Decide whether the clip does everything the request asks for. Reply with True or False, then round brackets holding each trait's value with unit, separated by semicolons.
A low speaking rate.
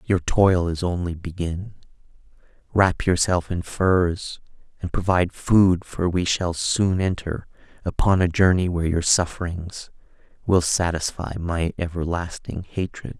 True (125 wpm)